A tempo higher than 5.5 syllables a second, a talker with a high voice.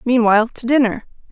Yes: 6.0 syllables/s; high, 235 Hz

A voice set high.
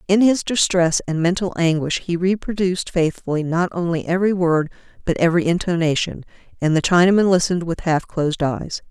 No: medium, 175 Hz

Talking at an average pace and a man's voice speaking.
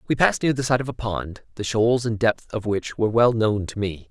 No: fast, 280 wpm; male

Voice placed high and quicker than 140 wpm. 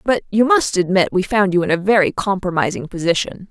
Yes: high, 195 Hz; fast, 205 wpm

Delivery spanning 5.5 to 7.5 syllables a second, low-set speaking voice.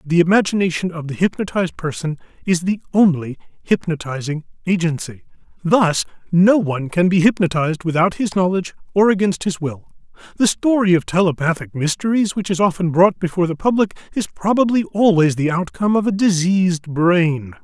No: 5.6 syllables/s; medium, 180 Hz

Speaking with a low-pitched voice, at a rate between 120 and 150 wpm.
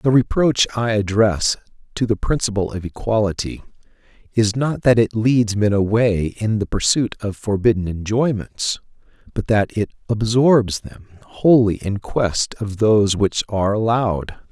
Yes: low, 110 Hz; average, 145 wpm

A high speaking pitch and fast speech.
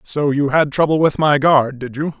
No: medium, 145 Hz; fast, 245 wpm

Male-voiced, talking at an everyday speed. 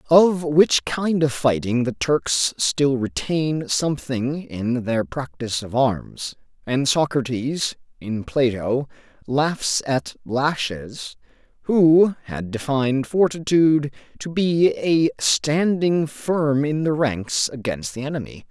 No: male; slow, 120 wpm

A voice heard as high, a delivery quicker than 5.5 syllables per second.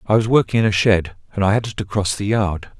No: low, 100 Hz; 5.7 syllables/s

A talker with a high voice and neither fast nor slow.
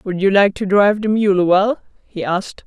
No: high, 200 Hz; fast, 225 wpm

